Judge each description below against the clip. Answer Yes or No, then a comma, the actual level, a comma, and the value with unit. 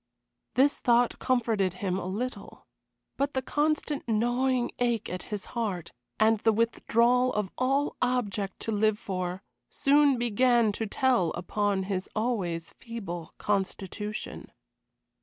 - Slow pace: Yes, slow, 125 wpm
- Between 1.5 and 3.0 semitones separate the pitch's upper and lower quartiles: No, average, 4.1 semitones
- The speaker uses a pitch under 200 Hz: No, high, 225 Hz